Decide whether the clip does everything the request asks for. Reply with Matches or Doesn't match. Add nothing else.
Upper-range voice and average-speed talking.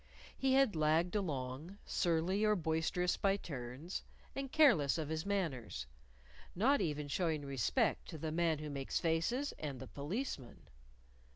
Doesn't match